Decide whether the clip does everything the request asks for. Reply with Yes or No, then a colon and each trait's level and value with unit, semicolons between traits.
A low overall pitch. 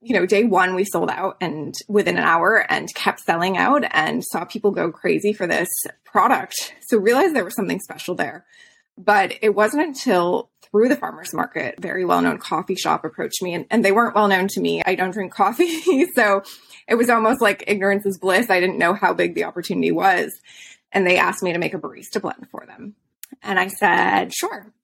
No: high, 205 Hz